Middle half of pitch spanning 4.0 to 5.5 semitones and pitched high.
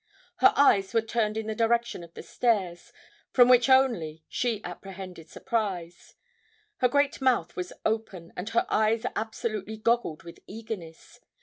Yes: average, 4.7 semitones; high, 220 Hz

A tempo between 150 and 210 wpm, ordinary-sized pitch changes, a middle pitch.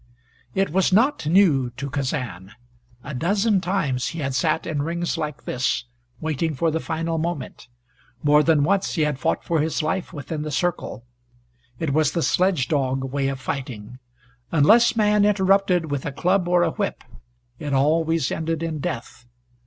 Yes: average, 170 wpm; average, 4.2 semitones; medium, 155 Hz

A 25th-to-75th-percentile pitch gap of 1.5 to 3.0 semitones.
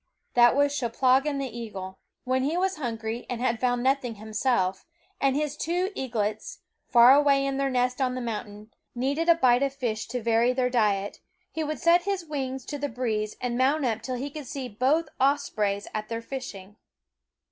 No: average, 3.5 semitones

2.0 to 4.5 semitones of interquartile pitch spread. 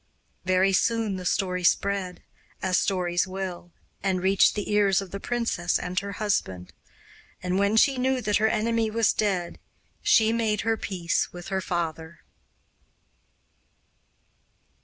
Yes: average, 3.0 semitones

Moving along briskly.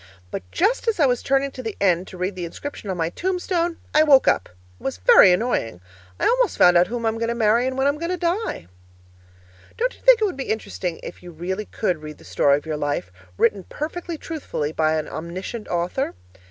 Yes: fast, 225 wpm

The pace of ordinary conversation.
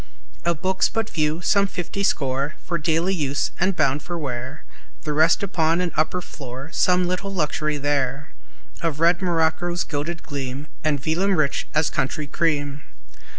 Yes: average, 155 wpm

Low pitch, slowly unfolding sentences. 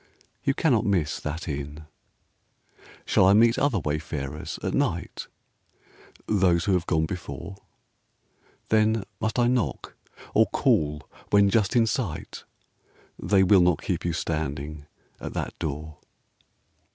Yes: very low, 90 Hz; slow, 125 wpm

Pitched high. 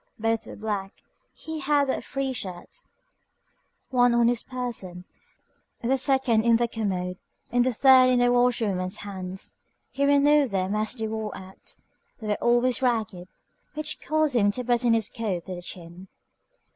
Yes: high, 235 Hz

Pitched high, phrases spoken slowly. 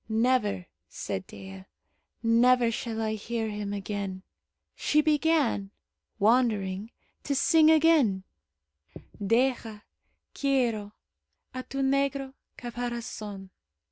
Yes: high, 230 Hz; slow, 90 wpm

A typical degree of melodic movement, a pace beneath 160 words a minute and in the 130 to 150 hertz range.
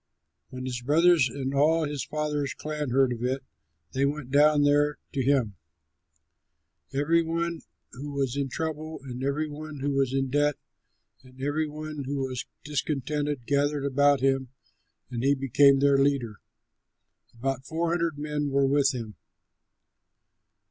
No: narrow, 2.0 semitones; average, 150 wpm; medium, 140 Hz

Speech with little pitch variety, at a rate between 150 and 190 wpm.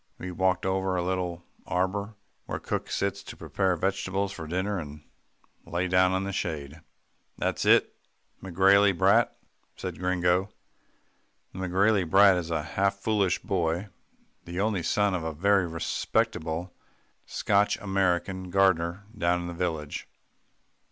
No: narrow, 2.1 semitones; average, 140 wpm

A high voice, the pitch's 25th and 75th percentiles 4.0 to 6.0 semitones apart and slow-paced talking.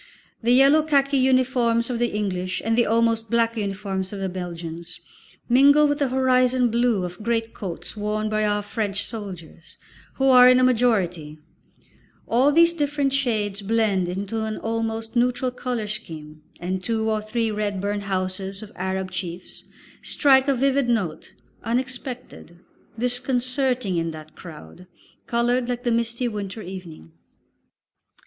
No: high, 225 Hz; average, 4.6 semitones; average, 145 wpm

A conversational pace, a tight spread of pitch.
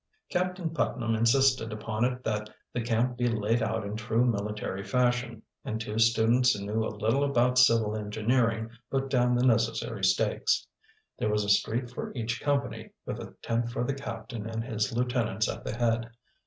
Yes: average, 180 wpm; narrow, 2.2 semitones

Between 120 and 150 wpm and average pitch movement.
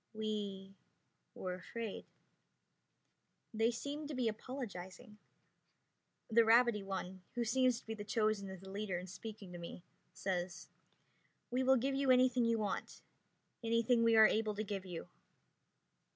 Yes: average, 140 wpm; average, 3.6 semitones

